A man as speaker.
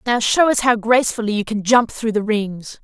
No: female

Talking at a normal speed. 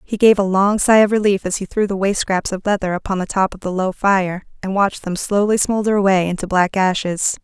No: fast, 250 wpm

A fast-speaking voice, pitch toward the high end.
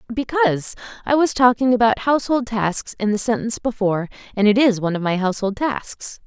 No: average, 180 wpm; high, 225 Hz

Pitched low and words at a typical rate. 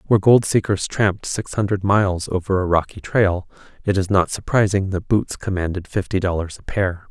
Yes: very low, 95 Hz; average, 185 wpm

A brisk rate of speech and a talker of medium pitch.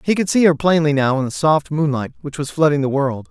Yes: fast, 270 wpm; medium, 150 Hz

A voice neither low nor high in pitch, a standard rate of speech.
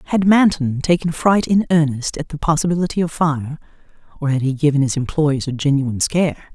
Yes: medium, 155 Hz; average, 185 wpm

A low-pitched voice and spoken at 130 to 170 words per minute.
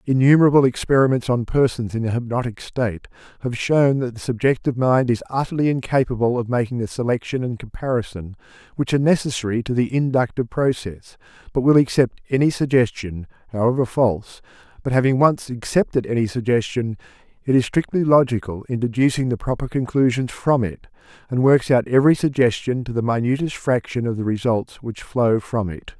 Yes: low, 125 Hz; average, 160 wpm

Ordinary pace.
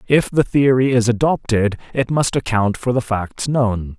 Yes: average, 180 wpm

